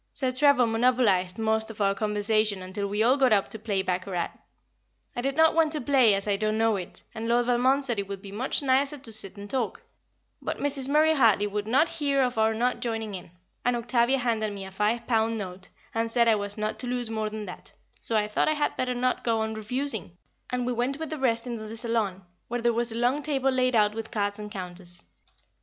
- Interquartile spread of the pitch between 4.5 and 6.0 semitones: No, average, 3.4 semitones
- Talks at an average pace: No, fast, 235 wpm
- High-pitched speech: Yes, high, 225 Hz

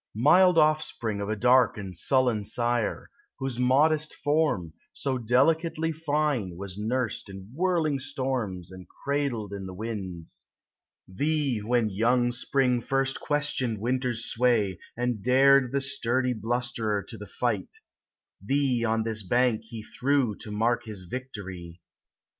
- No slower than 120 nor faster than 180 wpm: Yes, slow, 135 wpm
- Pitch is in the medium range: No, low, 120 Hz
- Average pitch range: Yes, average, 4.4 semitones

